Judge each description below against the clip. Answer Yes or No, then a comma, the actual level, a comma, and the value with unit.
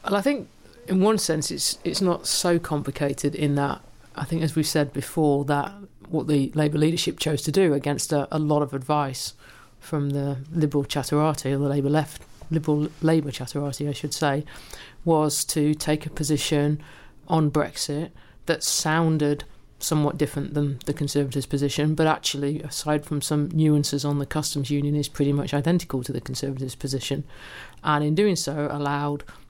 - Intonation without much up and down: Yes, narrow, 1.6 semitones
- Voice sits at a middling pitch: Yes, medium, 150 Hz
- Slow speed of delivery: No, average, 175 wpm